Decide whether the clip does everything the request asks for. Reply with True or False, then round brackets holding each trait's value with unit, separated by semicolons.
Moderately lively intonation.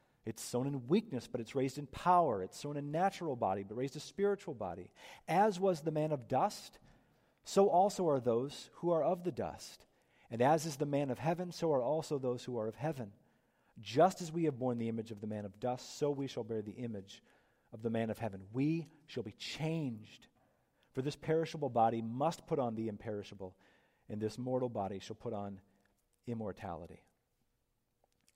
False (6.1 semitones)